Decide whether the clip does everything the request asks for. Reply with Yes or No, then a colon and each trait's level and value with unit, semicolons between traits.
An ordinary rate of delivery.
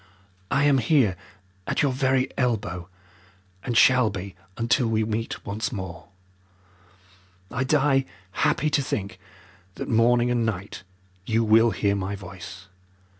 No: slow, 130 wpm